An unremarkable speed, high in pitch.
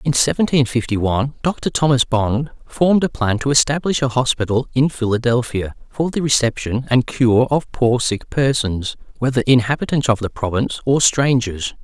No: average, 160 wpm; low, 125 Hz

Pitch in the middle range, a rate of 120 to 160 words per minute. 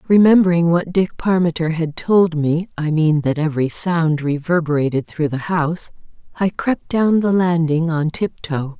Yes: medium, 165 Hz; average, 155 wpm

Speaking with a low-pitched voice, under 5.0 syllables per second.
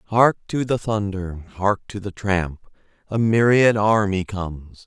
Yes: low, 100 Hz; 4.0 syllables/s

